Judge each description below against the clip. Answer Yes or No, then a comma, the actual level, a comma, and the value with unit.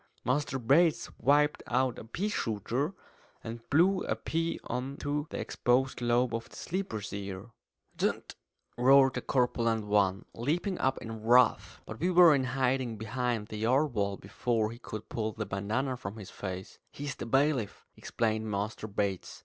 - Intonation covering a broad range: No, average, 4.2 semitones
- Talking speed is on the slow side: No, average, 165 wpm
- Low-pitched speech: Yes, low, 120 Hz